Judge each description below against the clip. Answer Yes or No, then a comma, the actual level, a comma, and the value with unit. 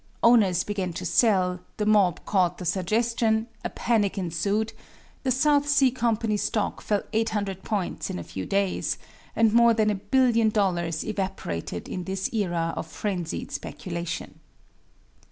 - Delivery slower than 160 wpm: Yes, average, 145 wpm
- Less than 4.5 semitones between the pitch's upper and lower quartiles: Yes, average, 3.7 semitones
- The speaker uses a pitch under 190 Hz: No, high, 205 Hz